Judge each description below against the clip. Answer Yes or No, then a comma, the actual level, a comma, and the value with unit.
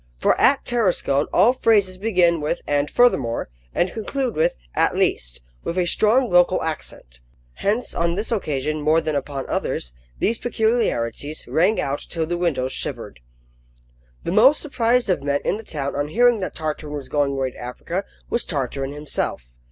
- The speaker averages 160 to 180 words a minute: Yes, average, 165 wpm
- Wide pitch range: Yes, wide, 7.2 semitones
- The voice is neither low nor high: Yes, medium, 170 Hz